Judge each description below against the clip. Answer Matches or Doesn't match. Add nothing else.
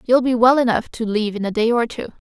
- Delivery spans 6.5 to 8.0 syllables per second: Matches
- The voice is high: Matches